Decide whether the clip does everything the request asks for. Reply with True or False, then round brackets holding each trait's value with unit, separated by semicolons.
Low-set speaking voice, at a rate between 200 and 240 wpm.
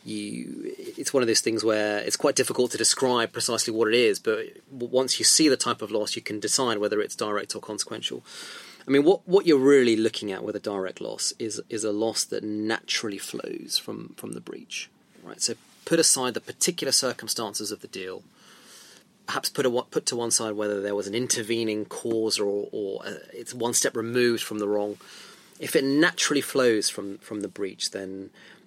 True (115 Hz; 205 wpm)